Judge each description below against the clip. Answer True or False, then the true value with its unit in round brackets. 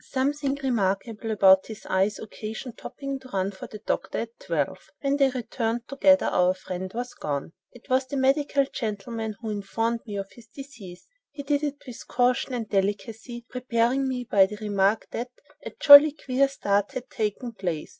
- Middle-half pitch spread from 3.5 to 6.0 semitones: True (4.6 semitones)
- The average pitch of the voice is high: True (230 Hz)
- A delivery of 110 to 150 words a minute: False (175 wpm)